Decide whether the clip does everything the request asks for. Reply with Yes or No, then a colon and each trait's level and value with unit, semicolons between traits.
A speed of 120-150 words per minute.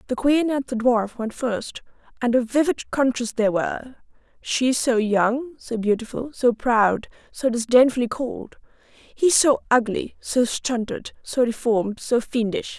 Yes: average, 145 wpm